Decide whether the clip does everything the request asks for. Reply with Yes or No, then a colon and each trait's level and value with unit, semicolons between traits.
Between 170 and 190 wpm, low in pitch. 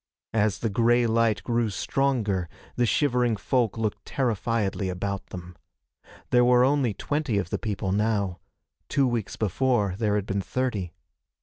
No: average, 145 wpm; low, 110 Hz